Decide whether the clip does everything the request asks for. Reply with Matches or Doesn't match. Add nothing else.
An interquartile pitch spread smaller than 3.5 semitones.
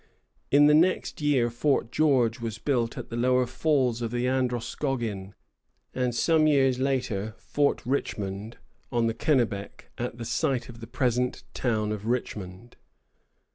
Matches